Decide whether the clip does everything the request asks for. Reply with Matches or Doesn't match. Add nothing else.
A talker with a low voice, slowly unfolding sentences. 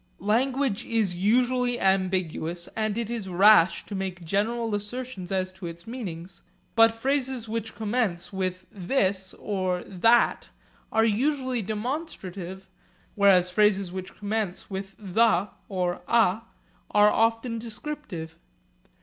Doesn't match